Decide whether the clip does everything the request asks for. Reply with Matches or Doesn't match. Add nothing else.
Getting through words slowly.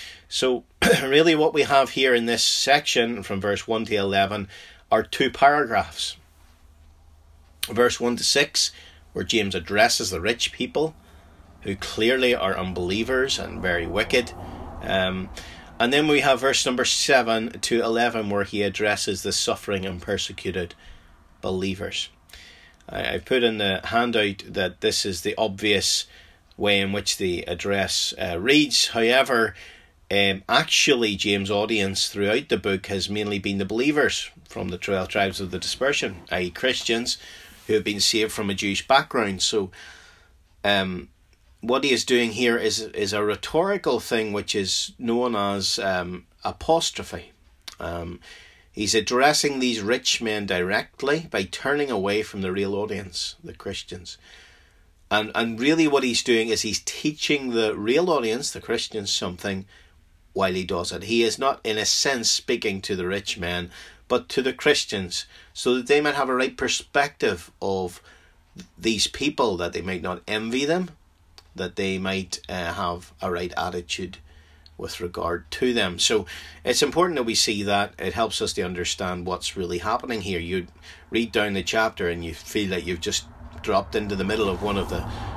Doesn't match